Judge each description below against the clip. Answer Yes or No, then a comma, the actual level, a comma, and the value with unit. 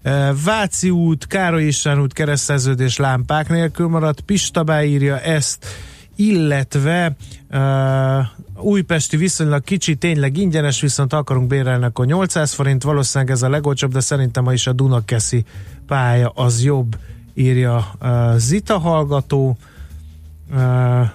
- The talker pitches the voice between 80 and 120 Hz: No, medium, 140 Hz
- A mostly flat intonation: No, average, 3.7 semitones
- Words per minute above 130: No, average, 115 wpm